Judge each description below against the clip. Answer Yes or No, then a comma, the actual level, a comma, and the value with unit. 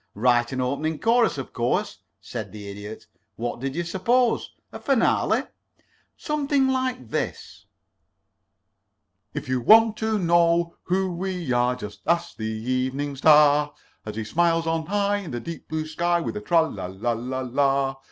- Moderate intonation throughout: No, wide, 6.6 semitones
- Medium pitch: Yes, medium, 155 Hz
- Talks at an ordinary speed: Yes, average, 155 wpm